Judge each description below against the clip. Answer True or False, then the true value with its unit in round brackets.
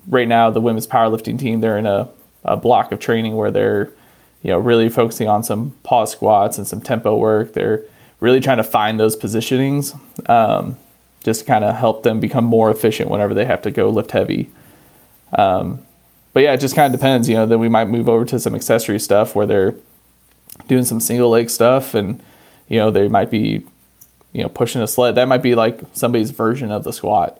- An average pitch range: False (2.0 semitones)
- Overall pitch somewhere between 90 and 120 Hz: True (115 Hz)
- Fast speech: True (210 wpm)